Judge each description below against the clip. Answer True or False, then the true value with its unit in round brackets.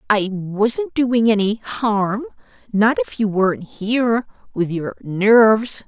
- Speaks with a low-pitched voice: False (215 Hz)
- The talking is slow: True (110 wpm)